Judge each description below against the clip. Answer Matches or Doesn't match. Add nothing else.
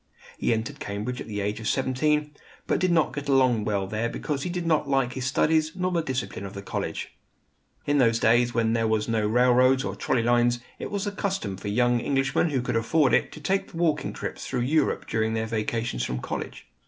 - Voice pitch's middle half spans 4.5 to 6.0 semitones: Matches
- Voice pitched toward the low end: Matches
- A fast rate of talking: Matches